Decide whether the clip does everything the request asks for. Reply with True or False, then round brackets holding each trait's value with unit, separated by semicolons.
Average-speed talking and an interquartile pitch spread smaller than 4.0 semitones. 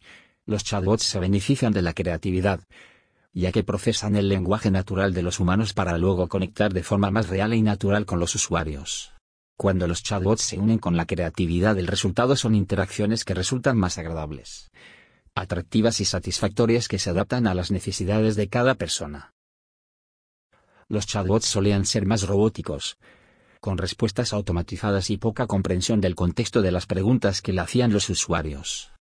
True (160 wpm; 3.0 semitones)